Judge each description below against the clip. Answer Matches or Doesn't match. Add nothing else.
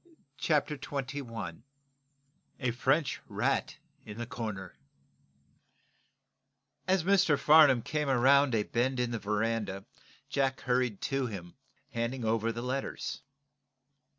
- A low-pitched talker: Matches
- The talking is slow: Matches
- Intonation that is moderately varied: Matches